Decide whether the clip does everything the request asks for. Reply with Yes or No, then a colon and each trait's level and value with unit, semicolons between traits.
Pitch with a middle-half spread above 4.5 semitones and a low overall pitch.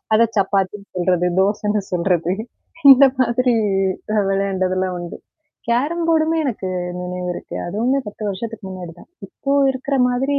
No: wide, 5.5 semitones; high, 205 Hz